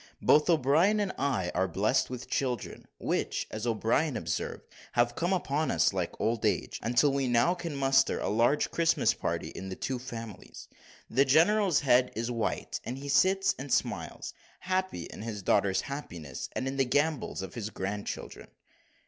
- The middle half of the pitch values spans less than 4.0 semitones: No, average, 5.2 semitones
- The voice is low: Yes, low, 130 Hz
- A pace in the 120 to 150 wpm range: No, average, 170 wpm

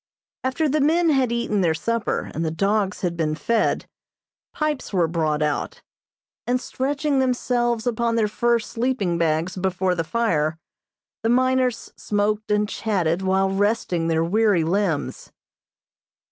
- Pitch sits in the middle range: No, high, 210 Hz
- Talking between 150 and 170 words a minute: No, average, 140 wpm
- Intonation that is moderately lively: No, wide, 5.8 semitones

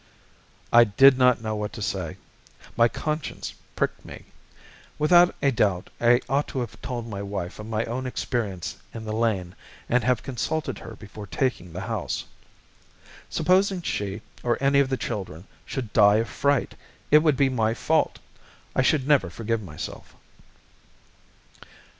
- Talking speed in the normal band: Yes, average, 155 wpm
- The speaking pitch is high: No, low, 115 Hz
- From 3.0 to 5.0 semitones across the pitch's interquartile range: Yes, average, 4.4 semitones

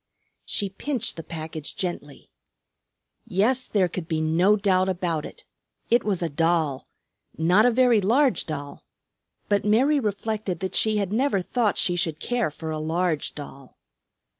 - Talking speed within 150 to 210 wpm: Yes, average, 155 wpm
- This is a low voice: No, medium, 185 Hz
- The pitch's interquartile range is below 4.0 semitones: No, average, 5.1 semitones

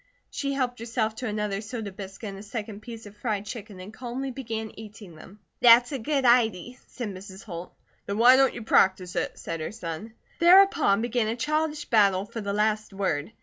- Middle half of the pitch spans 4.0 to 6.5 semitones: No, average, 3.5 semitones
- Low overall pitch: No, high, 220 Hz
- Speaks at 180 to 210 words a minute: Yes, average, 195 wpm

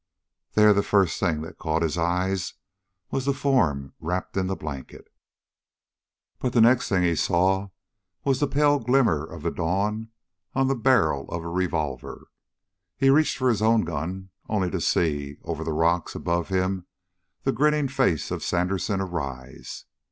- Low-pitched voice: Yes, very low, 95 Hz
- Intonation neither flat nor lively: No, wide, 5.9 semitones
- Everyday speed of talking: Yes, average, 160 wpm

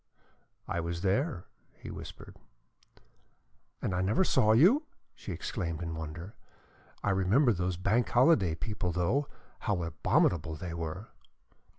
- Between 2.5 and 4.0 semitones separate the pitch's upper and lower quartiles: No, average, 5.2 semitones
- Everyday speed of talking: No, slow, 125 wpm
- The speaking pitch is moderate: No, very low, 95 Hz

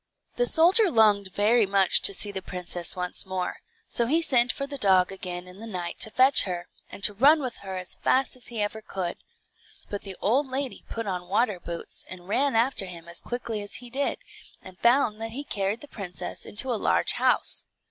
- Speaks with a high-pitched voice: Yes, high, 210 Hz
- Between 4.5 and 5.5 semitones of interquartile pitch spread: Yes, average, 5.1 semitones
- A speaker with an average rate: No, fast, 210 wpm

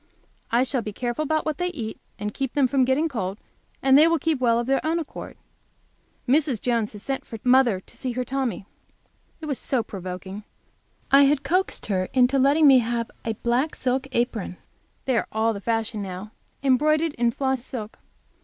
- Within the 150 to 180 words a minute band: No, average, 195 wpm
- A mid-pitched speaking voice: No, very high, 250 Hz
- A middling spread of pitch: Yes, average, 3.7 semitones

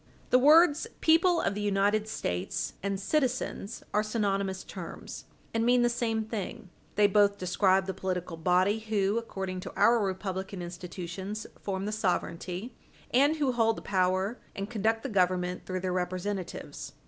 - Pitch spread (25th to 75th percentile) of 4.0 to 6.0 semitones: No, average, 3.4 semitones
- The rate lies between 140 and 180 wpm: Yes, average, 155 wpm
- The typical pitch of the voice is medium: No, high, 200 Hz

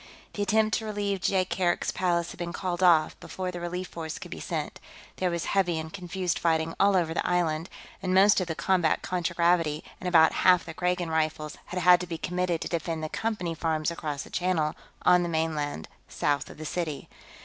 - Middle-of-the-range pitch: Yes, medium, 175 Hz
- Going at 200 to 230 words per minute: Yes, fast, 205 wpm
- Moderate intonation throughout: No, narrow, 2.3 semitones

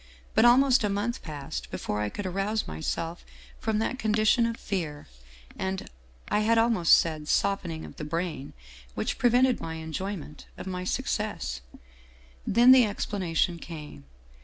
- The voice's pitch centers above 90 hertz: Yes, high, 190 Hz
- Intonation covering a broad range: Yes, wide, 6.0 semitones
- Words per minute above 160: No, average, 155 wpm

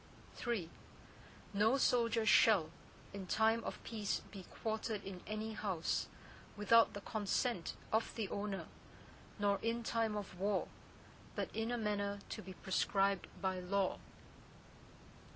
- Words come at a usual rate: No, slow, 130 wpm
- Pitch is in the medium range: No, high, 210 Hz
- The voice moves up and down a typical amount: No, narrow, 2.3 semitones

